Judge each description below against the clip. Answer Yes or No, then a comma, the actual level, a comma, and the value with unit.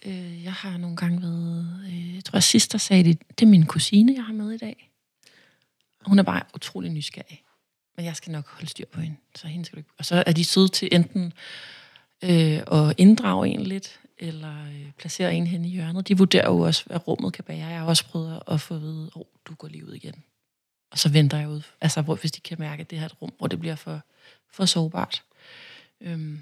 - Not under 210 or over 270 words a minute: Yes, fast, 225 wpm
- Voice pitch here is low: No, medium, 170 Hz